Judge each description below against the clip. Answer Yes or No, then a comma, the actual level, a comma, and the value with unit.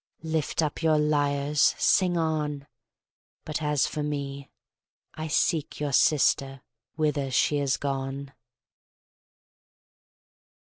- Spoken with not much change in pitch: Yes, narrow, 1.8 semitones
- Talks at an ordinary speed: No, slow, 100 wpm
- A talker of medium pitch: Yes, medium, 145 Hz